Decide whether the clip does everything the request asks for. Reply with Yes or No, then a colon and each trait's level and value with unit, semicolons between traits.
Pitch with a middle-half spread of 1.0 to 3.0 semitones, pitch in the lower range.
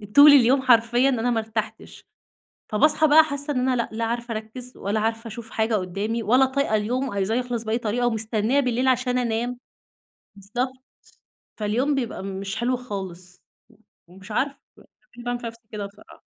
No: average, 2.7 semitones; high, 235 Hz